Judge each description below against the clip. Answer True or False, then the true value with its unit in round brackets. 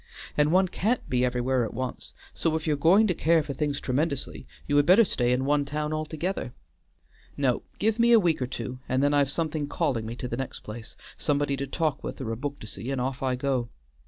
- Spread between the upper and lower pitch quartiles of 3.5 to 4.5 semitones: True (3.9 semitones)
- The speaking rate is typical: False (230 wpm)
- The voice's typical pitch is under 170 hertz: True (140 Hz)